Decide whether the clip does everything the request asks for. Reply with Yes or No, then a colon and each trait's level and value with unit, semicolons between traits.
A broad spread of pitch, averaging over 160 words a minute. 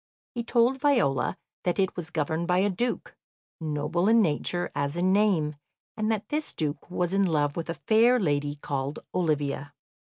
Yes: wide, 6.2 semitones; average, 170 wpm